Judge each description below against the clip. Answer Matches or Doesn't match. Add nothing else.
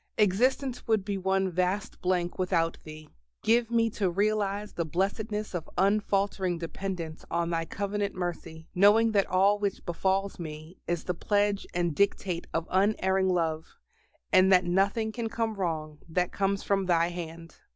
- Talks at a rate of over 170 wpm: Doesn't match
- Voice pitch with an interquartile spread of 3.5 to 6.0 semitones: Doesn't match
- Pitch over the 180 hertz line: Matches